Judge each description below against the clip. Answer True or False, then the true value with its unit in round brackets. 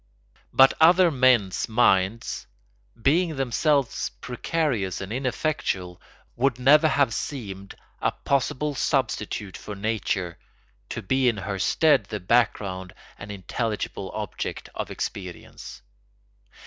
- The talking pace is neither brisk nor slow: False (110 wpm)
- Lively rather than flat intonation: True (5.8 semitones)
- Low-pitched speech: True (115 Hz)